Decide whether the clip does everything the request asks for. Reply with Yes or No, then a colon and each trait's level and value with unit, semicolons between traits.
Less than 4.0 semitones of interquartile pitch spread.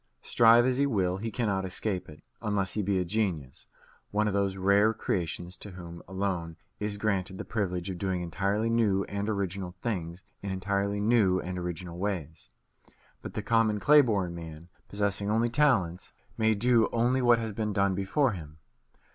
Yes: average, 3.3 semitones